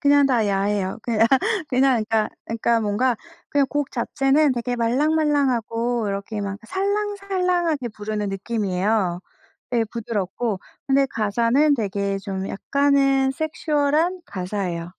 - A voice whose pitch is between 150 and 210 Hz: No, high, 235 Hz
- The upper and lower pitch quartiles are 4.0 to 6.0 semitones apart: Yes, wide, 5.6 semitones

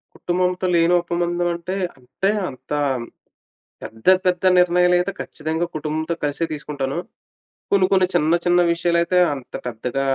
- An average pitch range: Yes, average, 3.0 semitones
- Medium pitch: Yes, medium, 170 Hz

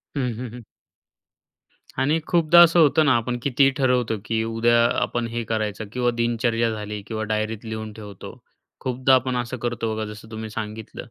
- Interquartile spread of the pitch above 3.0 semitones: No, narrow, 2.5 semitones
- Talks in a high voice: No, low, 115 Hz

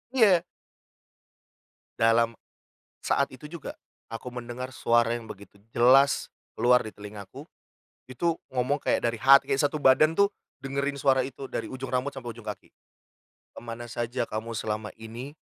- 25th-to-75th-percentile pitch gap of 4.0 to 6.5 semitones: No, average, 3.0 semitones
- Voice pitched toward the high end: No, low, 125 Hz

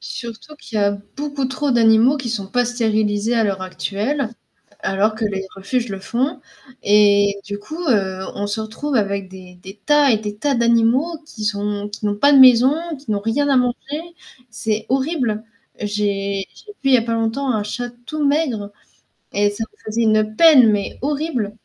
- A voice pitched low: No, high, 225 Hz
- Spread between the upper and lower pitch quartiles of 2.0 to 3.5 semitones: No, average, 4.3 semitones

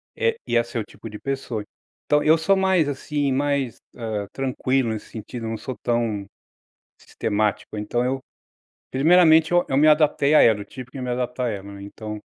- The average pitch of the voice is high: No, low, 125 Hz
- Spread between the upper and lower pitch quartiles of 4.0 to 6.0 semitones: Yes, average, 4.8 semitones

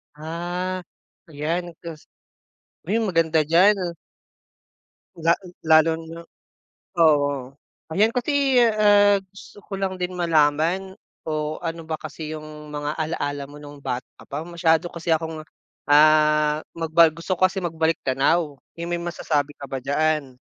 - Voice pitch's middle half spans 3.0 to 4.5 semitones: No, narrow, 2.6 semitones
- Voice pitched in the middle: Yes, medium, 160 Hz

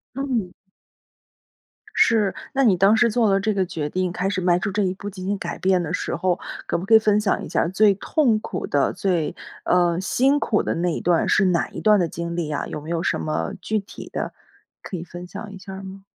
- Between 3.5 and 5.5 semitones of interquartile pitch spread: No, average, 3.1 semitones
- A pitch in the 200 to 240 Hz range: No, high, 190 Hz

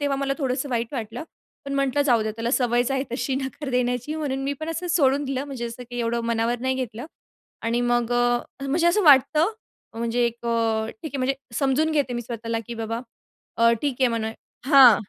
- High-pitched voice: Yes, very high, 250 Hz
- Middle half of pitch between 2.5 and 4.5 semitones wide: Yes, average, 3.0 semitones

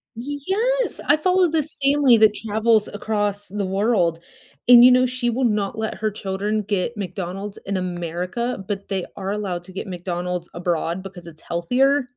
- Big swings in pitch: No, average, 4.8 semitones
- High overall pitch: Yes, high, 205 Hz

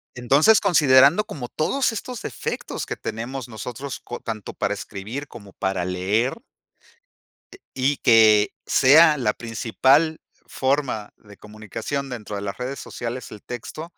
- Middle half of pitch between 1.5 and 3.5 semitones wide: No, average, 4.8 semitones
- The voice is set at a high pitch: No, low, 125 Hz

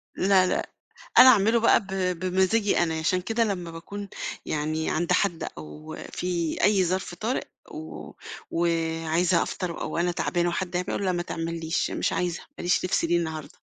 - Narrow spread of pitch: Yes, narrow, 2.3 semitones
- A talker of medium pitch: Yes, medium, 175 Hz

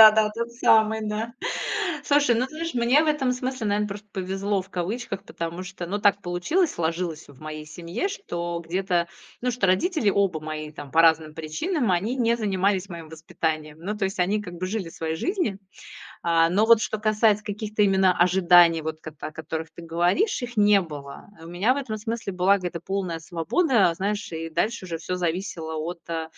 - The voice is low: No, high, 190 Hz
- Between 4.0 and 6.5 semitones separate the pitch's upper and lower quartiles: Yes, average, 4.6 semitones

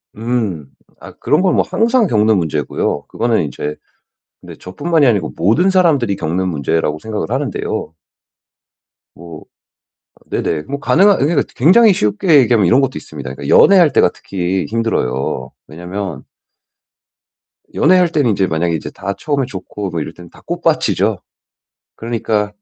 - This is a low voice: Yes, low, 105 Hz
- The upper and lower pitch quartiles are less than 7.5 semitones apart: No, wide, 8.9 semitones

